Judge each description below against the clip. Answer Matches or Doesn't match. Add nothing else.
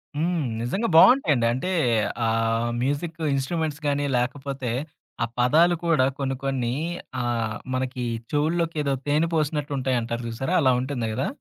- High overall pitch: Doesn't match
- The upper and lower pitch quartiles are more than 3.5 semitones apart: Matches